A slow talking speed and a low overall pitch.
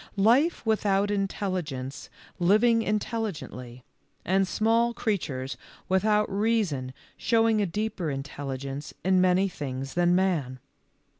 No: slow, 100 wpm; high, 190 Hz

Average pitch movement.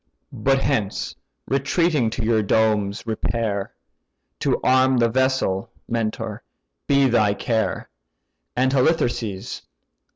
Yes: average, 3.6 semitones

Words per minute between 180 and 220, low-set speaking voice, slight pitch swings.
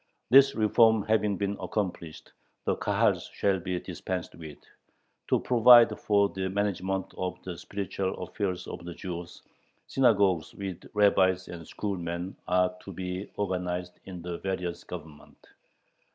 No: slow, 135 wpm; very low, 95 Hz; narrow, 2.3 semitones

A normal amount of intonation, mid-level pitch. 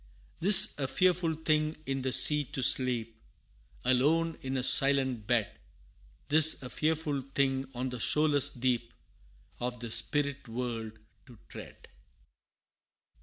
No: average, 3.6 semitones; low, 130 Hz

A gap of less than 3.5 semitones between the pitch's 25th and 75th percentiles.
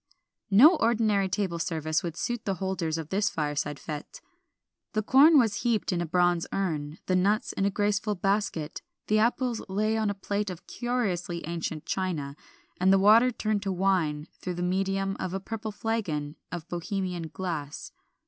No: average, 4.0 semitones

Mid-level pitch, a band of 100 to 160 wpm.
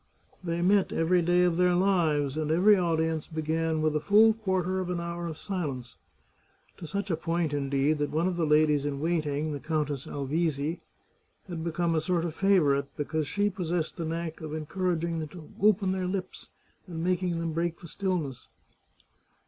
No: medium, 165 Hz; average, 190 wpm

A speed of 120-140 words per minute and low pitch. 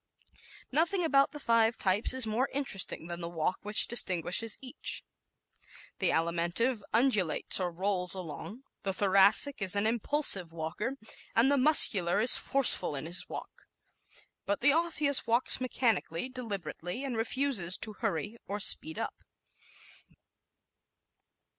No: slow, 135 wpm; high, 215 Hz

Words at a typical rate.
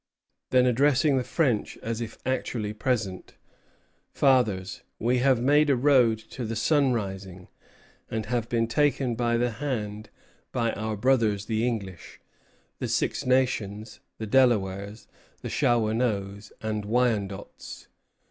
No: slow, 125 wpm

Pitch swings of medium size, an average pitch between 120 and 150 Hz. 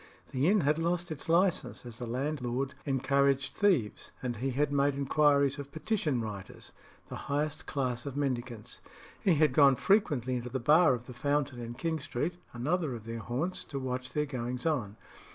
Yes: average, 3.6 semitones; medium, 140 Hz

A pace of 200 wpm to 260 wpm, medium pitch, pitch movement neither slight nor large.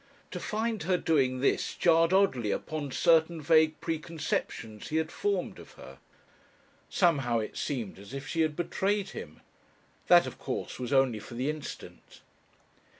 No: average, 150 wpm; medium, 155 Hz; average, 4.7 semitones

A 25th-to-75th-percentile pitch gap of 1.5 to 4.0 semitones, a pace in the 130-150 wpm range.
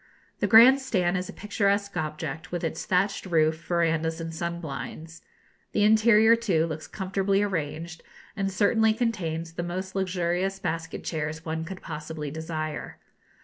Yes: average, 3.6 semitones; average, 145 wpm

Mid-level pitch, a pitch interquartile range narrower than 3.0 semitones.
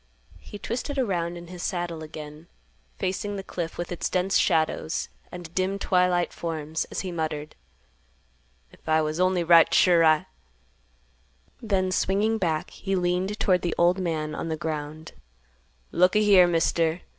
Yes: medium, 175 Hz; narrow, 2.6 semitones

